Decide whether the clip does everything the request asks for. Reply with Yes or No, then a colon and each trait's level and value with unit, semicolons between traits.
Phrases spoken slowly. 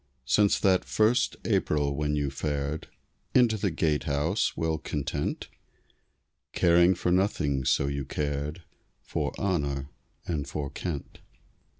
Yes: slow, 115 wpm